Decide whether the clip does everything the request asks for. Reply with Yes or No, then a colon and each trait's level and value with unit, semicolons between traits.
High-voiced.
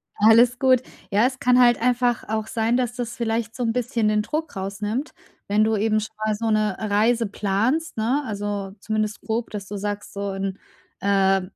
Yes: high, 220 Hz